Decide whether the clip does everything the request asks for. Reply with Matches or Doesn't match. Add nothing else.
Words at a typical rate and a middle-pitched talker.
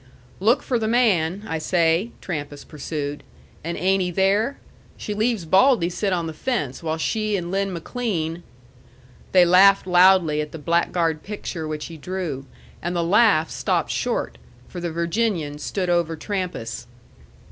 Matches